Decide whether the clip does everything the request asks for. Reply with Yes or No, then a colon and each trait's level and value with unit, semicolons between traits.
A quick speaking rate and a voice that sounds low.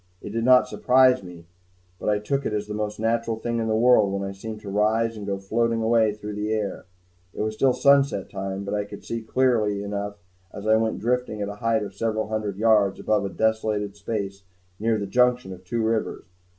Yes: fast, 225 wpm; low, 110 Hz